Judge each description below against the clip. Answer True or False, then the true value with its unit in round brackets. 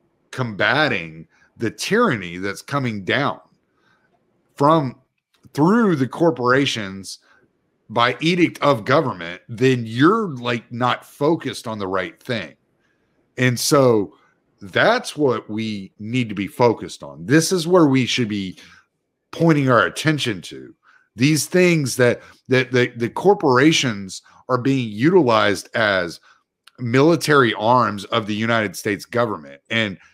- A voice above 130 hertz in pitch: False (125 Hz)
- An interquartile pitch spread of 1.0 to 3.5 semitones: False (4.7 semitones)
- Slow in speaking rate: True (125 wpm)